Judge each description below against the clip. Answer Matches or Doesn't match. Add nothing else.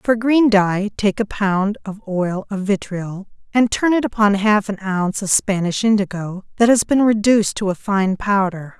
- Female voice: Matches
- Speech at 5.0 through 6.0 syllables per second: Doesn't match